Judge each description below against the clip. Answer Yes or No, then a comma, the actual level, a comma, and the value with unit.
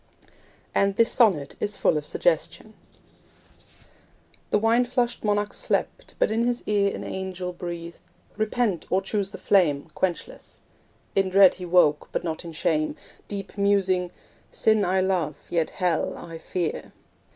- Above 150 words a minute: No, average, 145 wpm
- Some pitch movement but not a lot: Yes, average, 3.4 semitones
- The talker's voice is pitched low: No, high, 190 Hz